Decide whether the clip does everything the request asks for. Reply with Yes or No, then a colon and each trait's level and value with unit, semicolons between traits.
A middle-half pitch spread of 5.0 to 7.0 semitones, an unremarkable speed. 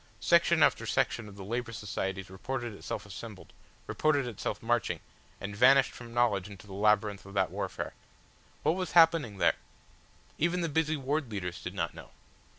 Yes: wide, 5.6 semitones; average, 165 wpm